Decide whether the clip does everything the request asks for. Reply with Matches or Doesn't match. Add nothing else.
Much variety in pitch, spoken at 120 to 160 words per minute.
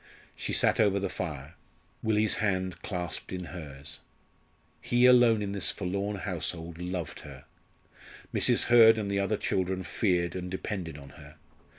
Doesn't match